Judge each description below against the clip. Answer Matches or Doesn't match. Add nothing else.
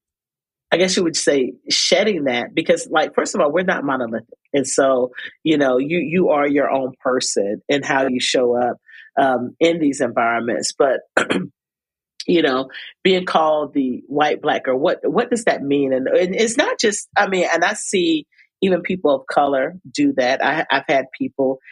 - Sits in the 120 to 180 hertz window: Matches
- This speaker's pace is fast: Doesn't match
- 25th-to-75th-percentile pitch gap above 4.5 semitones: Matches